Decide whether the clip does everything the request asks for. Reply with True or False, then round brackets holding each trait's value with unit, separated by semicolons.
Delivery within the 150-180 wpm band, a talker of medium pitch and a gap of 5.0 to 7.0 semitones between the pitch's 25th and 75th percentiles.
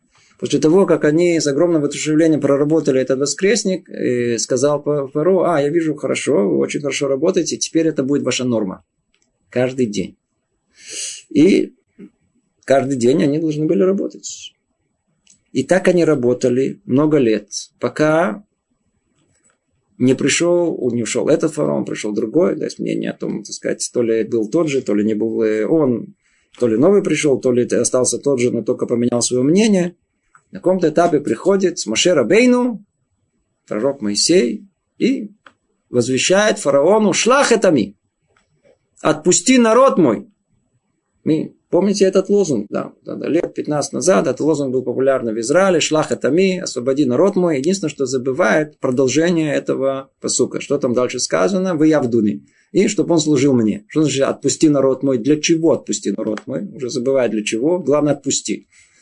True (155 wpm; 145 Hz; 5.4 semitones)